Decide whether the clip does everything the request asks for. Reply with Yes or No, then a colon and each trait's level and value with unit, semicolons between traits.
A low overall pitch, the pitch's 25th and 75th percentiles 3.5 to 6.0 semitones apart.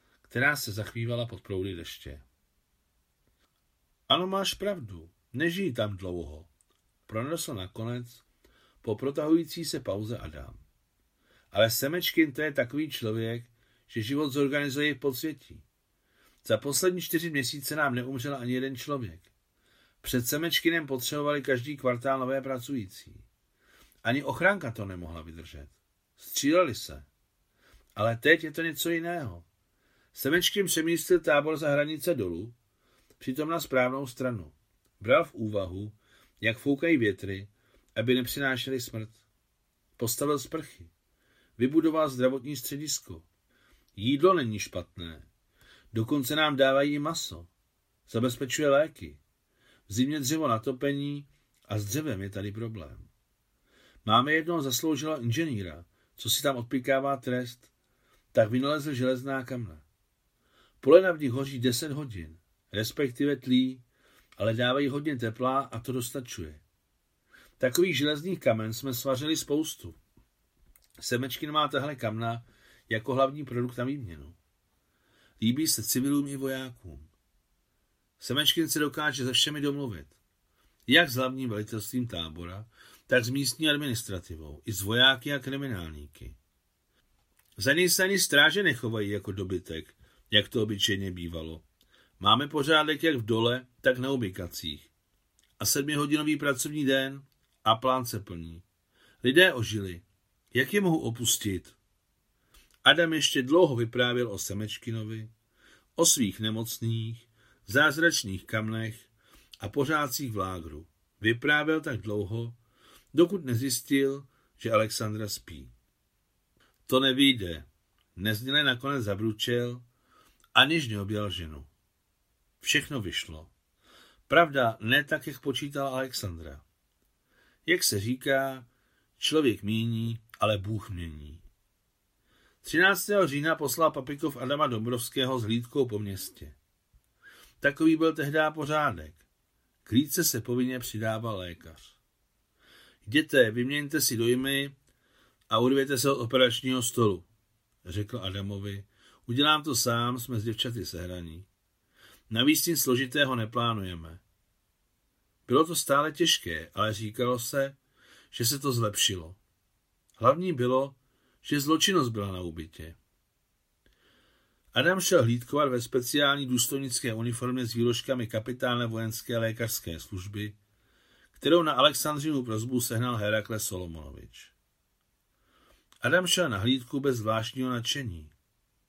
Yes: low, 120 Hz; wide, 5.6 semitones